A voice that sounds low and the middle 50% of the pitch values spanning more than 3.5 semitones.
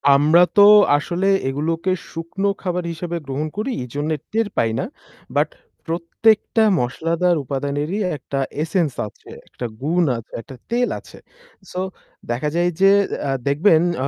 No: medium, 165 Hz; average, 4.1 semitones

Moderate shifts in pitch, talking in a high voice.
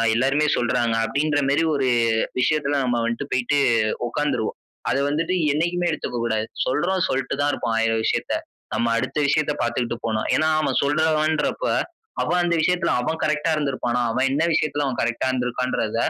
No: average, 4.1 semitones; medium, 140 Hz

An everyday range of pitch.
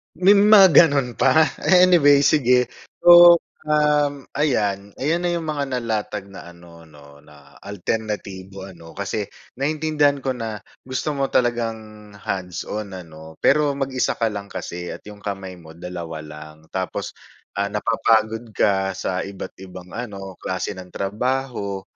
No: wide, 6.7 semitones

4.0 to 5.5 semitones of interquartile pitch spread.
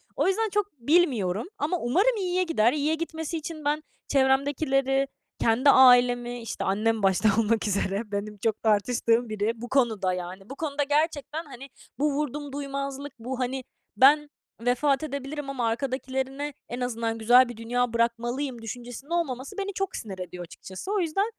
Yes: average, 4.5 semitones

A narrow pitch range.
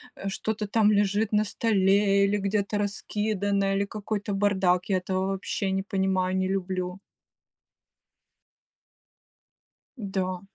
Yes: narrow, 1.4 semitones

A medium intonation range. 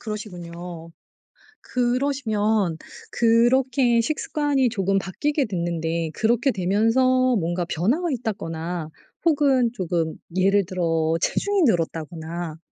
No: wide, 6.5 semitones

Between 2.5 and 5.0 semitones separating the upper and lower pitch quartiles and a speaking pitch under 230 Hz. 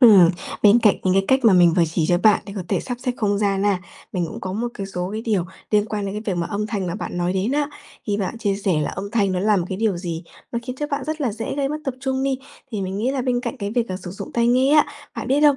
Yes: average, 4.4 semitones; high, 210 Hz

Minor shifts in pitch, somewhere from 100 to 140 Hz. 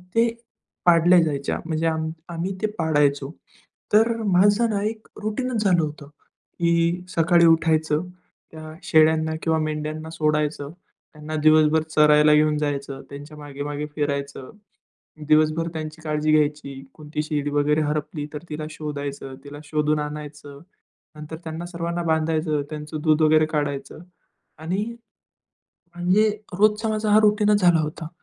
No: narrow, 2.1 semitones; medium, 155 Hz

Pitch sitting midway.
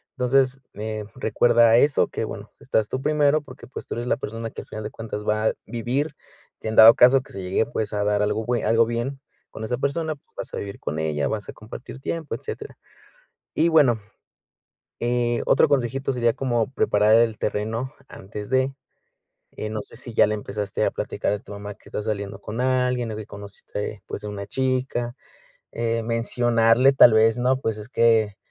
No: low, 115 Hz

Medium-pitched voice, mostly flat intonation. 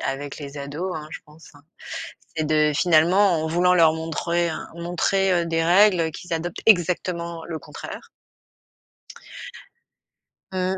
Yes: medium, 170 Hz; narrow, 2.3 semitones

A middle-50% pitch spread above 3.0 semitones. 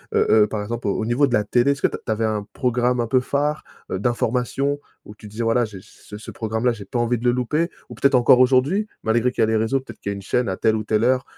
No: average, 2.7 semitones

